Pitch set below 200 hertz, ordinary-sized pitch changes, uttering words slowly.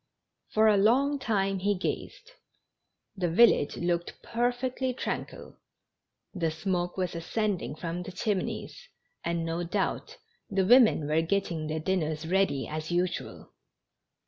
Yes: medium, 185 Hz; average, 4.6 semitones; slow, 125 wpm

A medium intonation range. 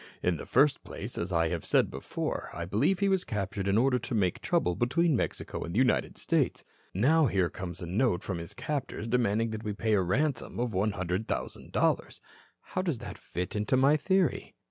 No: wide, 6.3 semitones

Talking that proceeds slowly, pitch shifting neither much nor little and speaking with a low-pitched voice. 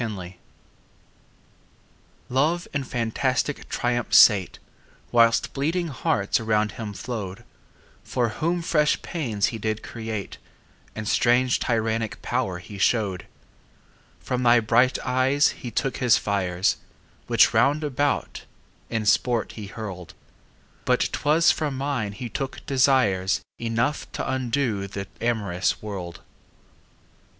Yes: slow, 120 wpm; average, 4.1 semitones; low, 115 Hz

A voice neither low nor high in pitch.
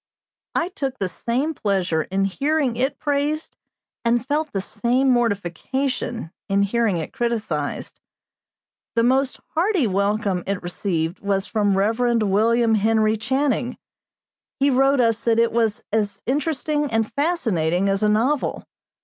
No: high, 230 Hz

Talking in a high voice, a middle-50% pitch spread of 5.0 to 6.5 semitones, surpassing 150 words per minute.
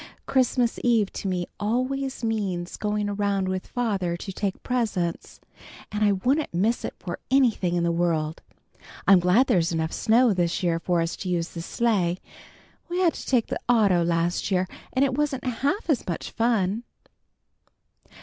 Yes: high, 200 Hz; wide, 5.6 semitones; average, 170 wpm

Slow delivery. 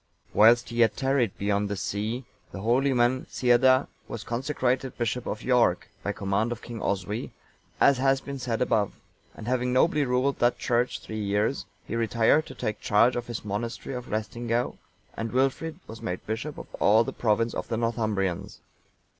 No: average, 175 wpm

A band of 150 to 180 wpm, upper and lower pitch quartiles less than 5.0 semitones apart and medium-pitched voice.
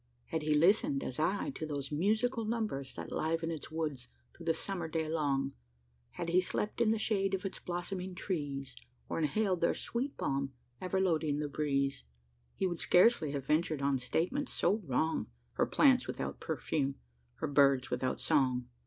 No: average, 170 wpm; wide, 5.5 semitones; medium, 160 Hz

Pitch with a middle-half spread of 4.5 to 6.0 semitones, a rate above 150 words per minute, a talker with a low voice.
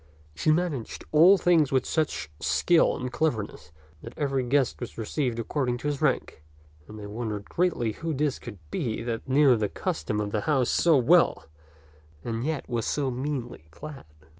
Yes: average, 5.1 semitones; average, 170 wpm; low, 130 Hz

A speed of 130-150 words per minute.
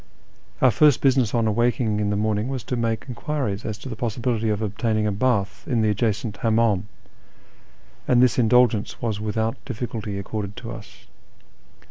No: average, 165 wpm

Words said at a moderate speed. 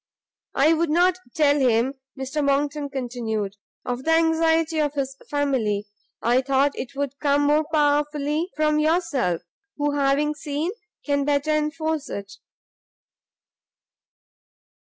No: slow, 120 wpm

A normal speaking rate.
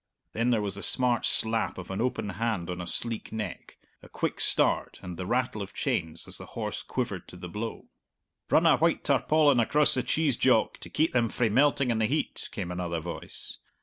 No: fast, 210 wpm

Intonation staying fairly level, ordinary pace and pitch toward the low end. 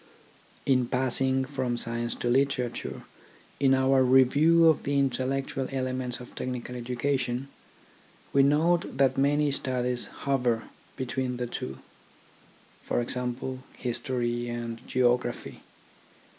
No: narrow, 1.9 semitones; slow, 110 wpm; low, 130 Hz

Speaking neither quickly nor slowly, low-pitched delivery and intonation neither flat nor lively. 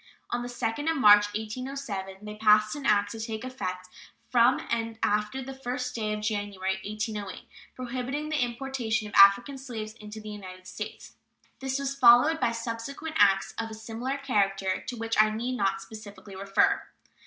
No: average, 170 wpm; high, 225 Hz; average, 3.5 semitones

